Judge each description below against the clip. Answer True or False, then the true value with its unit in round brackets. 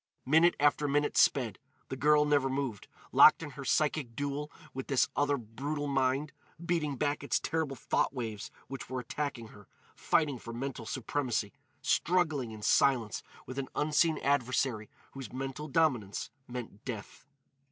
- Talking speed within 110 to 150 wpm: True (145 wpm)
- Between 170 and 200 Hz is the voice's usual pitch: False (135 Hz)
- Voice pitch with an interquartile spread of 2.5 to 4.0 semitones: True (3.1 semitones)